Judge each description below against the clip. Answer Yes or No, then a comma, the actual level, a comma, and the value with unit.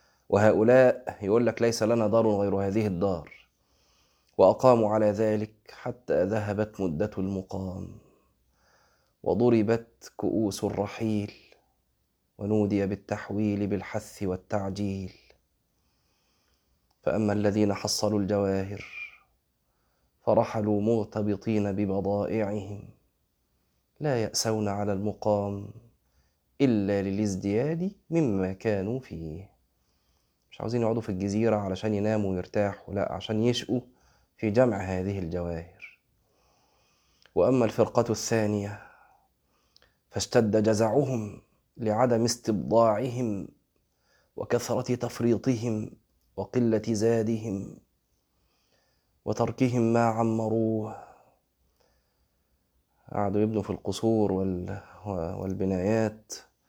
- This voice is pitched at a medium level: No, low, 105 Hz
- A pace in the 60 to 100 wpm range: Yes, average, 75 wpm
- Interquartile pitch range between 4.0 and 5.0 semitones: No, average, 2.7 semitones